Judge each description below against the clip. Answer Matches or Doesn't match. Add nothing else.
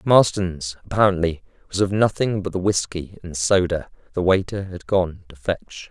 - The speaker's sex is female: Doesn't match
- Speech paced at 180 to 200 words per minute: Doesn't match